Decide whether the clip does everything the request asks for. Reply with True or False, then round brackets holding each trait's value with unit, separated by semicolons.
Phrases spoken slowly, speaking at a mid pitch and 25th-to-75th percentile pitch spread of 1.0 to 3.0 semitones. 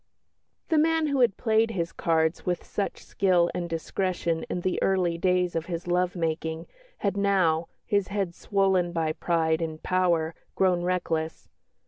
False (155 wpm; 180 Hz; 2.7 semitones)